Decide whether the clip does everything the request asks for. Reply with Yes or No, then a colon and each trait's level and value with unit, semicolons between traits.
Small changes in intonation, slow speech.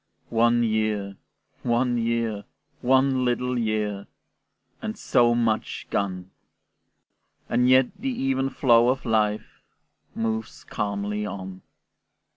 No: average, 3.1 semitones; slow, 100 wpm